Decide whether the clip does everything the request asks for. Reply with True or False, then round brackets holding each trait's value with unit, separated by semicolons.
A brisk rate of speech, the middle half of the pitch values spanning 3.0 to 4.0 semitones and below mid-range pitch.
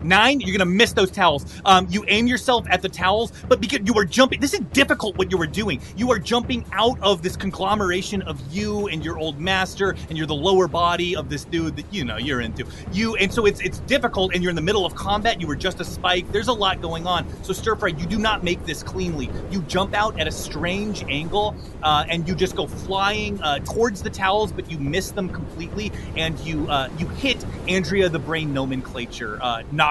False (235 wpm; 3.7 semitones; 190 Hz)